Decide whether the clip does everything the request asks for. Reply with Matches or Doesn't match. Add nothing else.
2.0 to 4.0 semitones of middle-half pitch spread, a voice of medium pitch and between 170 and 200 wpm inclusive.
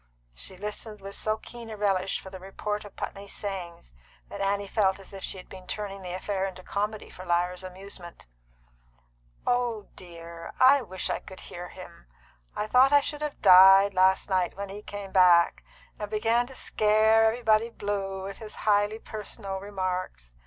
Doesn't match